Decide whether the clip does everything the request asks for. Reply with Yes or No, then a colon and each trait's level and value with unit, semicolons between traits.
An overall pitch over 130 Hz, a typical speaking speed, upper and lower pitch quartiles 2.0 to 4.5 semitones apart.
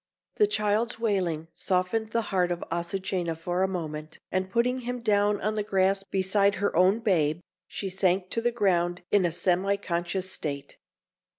Yes: high, 190 Hz; average, 170 wpm; average, 2.9 semitones